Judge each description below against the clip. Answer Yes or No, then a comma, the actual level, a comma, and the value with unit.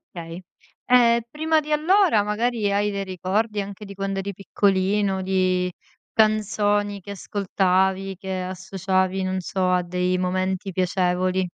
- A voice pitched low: No, high, 195 Hz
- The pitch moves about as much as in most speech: No, narrow, 1.9 semitones